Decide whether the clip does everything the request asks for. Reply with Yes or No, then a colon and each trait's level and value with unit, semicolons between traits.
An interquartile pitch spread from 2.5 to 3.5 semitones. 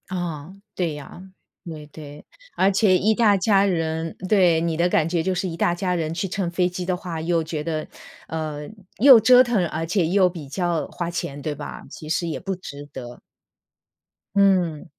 Yes: average, 2.9 semitones